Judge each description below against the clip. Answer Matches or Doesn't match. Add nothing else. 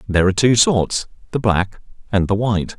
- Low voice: Matches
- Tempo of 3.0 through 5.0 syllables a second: Doesn't match